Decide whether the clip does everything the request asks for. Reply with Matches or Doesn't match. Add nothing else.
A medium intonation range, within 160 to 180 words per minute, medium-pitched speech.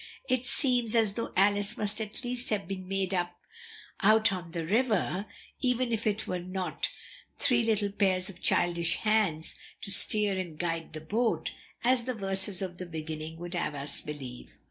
Doesn't match